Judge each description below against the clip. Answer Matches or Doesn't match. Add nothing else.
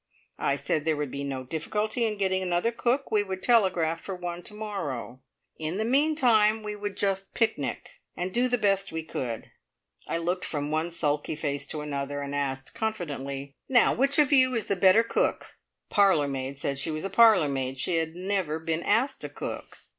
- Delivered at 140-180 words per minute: Doesn't match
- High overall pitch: Doesn't match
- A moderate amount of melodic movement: Doesn't match